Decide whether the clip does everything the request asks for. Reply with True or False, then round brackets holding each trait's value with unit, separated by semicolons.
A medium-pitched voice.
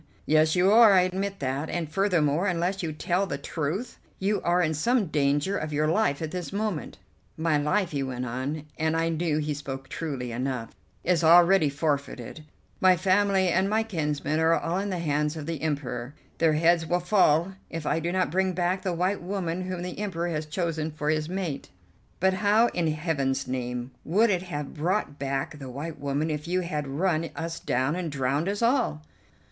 True (165 Hz)